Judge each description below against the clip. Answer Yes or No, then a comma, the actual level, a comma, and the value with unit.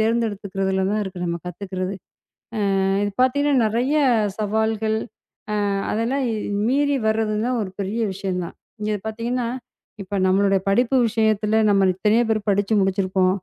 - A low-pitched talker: No, high, 210 Hz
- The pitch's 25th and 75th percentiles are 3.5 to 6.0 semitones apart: No, average, 2.9 semitones